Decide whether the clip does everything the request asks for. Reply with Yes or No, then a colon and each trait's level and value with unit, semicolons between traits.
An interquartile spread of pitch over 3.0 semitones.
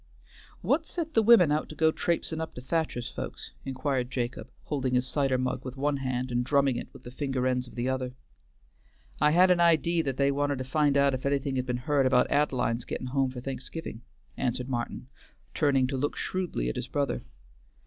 No: narrow, 2.6 semitones